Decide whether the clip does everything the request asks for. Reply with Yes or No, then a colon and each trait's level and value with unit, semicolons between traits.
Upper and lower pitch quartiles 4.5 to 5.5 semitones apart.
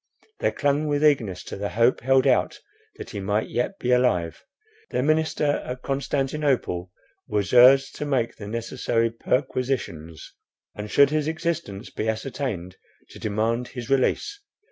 Yes: average, 4.9 semitones